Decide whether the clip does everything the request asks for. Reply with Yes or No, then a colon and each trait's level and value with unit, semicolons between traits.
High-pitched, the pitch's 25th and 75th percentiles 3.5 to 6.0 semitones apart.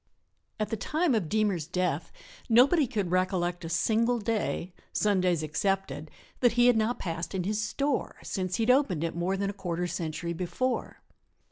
Yes: high, 195 Hz; average, 4.6 semitones